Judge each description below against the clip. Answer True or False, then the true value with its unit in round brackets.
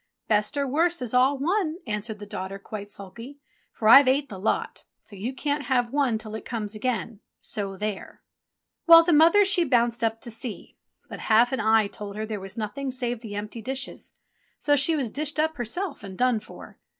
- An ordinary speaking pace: False (210 wpm)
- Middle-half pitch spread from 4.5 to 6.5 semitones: True (4.9 semitones)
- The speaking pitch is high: True (235 Hz)